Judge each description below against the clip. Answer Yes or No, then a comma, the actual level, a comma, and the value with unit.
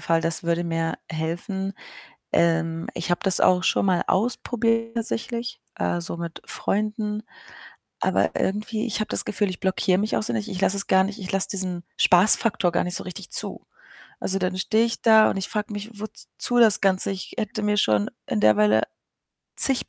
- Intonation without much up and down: No, average, 3.8 semitones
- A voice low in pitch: No, high, 195 Hz